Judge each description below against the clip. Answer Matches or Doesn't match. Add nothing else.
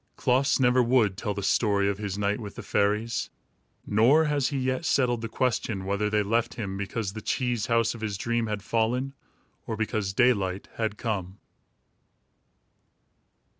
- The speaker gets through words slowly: Doesn't match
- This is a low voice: Matches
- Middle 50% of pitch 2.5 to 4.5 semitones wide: Matches